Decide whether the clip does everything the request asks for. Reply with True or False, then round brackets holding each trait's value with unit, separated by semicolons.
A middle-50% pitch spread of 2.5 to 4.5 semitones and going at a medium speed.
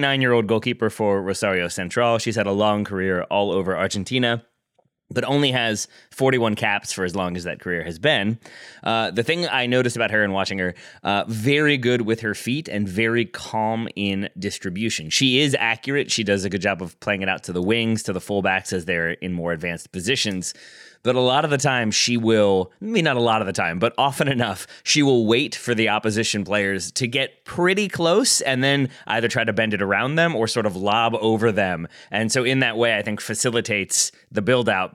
False (4.2 semitones; 215 wpm)